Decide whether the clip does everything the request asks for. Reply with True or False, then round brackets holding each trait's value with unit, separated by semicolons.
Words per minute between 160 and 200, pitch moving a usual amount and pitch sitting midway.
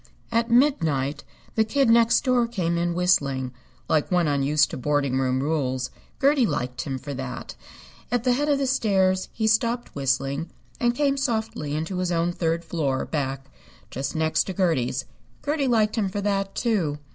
False (170 wpm; 8.6 semitones; 175 Hz)